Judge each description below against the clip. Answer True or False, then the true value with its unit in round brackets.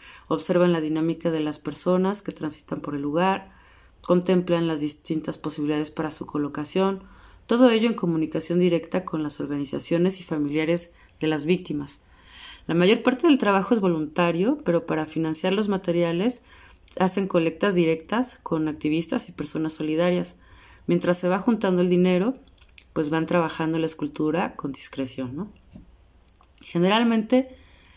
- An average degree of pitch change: True (3.3 semitones)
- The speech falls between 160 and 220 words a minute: False (140 wpm)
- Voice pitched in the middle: True (170 Hz)